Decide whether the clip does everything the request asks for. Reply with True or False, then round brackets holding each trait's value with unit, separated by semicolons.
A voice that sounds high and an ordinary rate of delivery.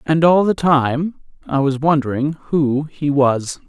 False (145 Hz; 165 wpm)